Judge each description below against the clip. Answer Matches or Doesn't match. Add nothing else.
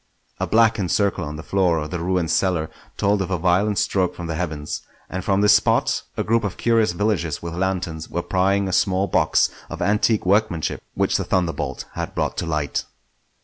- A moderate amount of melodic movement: Matches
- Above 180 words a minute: Matches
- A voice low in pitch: Matches